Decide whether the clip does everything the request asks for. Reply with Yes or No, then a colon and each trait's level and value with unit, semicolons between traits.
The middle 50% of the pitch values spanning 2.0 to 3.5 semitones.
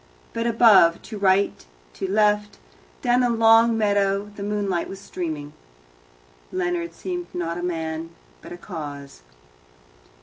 No: average, 4.2 semitones